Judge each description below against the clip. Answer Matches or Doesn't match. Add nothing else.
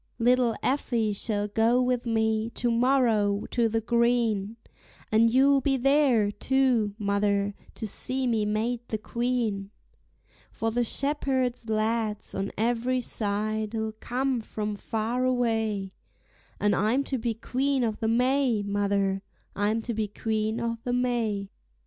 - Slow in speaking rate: Matches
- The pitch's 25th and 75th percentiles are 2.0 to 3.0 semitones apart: Matches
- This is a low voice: Doesn't match